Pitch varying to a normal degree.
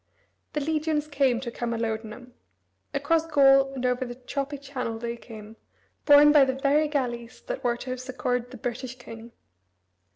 Yes: average, 3.0 semitones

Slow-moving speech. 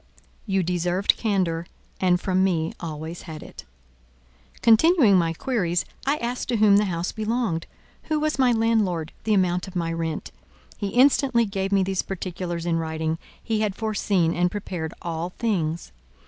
No: average, 160 wpm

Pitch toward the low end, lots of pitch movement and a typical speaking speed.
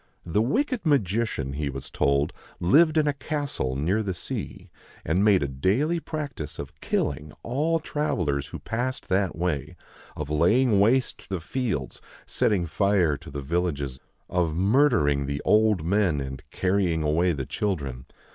Yes: very low, 90 Hz; wide, 8.2 semitones; average, 150 wpm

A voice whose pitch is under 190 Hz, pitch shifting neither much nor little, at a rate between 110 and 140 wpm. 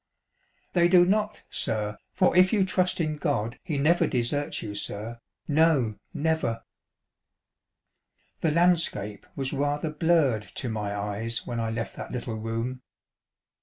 No: medium, 140 Hz; wide, 6.7 semitones; slow, 135 wpm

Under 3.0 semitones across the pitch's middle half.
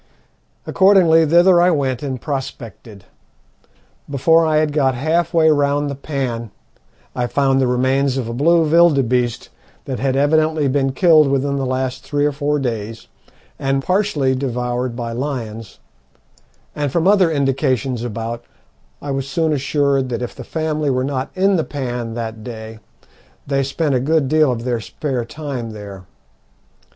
No: average, 3.7 semitones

